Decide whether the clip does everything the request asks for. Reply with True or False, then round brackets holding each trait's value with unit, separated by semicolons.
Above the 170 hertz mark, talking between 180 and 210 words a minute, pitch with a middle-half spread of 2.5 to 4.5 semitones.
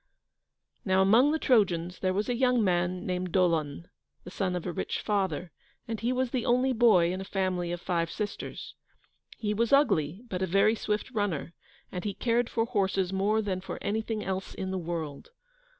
True (190 Hz; 190 wpm; 3.8 semitones)